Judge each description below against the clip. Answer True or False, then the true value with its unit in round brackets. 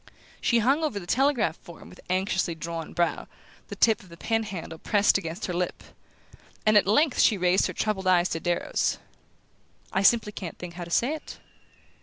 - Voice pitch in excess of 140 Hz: True (190 Hz)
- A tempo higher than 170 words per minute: True (190 wpm)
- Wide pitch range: False (4.1 semitones)